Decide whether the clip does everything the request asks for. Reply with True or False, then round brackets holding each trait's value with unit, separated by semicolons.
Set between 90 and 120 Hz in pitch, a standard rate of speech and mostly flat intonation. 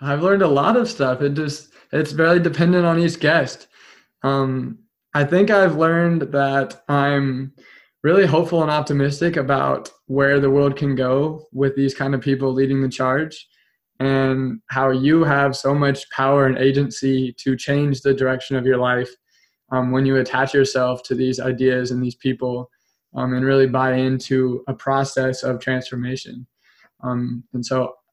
False (135 Hz; 165 wpm; 1.8 semitones)